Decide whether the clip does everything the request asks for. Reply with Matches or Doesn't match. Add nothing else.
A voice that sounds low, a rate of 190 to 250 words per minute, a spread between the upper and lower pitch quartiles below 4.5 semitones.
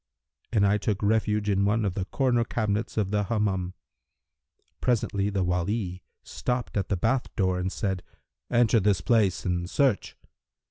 Doesn't match